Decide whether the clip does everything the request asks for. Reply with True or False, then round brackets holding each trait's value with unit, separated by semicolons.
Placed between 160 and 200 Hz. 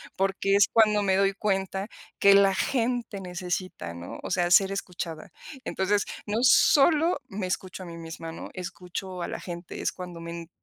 True (190 Hz)